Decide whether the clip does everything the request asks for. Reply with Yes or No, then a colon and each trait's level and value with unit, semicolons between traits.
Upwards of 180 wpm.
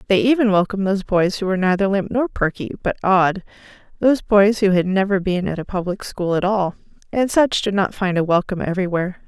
Yes: fast, 205 wpm